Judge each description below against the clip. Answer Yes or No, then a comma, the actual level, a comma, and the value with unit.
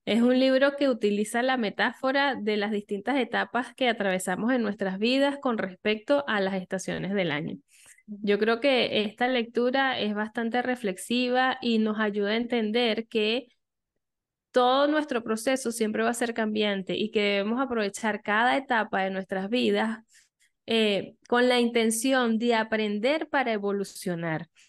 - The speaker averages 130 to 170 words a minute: Yes, average, 150 wpm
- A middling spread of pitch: Yes, average, 3.2 semitones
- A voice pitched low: No, high, 225 Hz